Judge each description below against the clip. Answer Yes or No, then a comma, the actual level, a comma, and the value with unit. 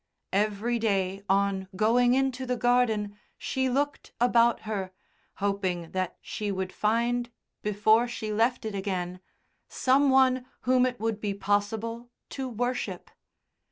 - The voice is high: Yes, high, 220 Hz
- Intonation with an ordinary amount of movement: Yes, average, 3.6 semitones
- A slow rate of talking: Yes, slow, 130 wpm